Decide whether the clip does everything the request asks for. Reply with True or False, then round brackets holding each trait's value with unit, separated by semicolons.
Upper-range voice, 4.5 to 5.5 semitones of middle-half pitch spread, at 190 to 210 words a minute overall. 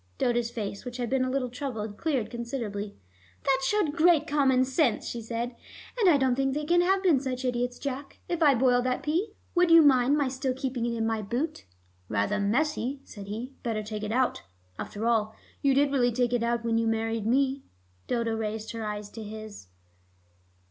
False (245 Hz; 3.5 semitones; 195 wpm)